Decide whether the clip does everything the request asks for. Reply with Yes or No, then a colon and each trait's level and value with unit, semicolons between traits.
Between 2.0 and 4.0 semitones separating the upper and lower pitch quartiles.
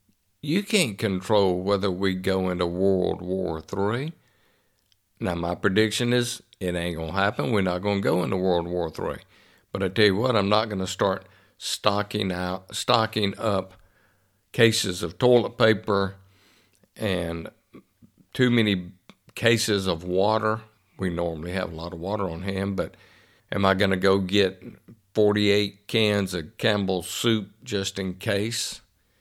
Yes: narrow, 2.6 semitones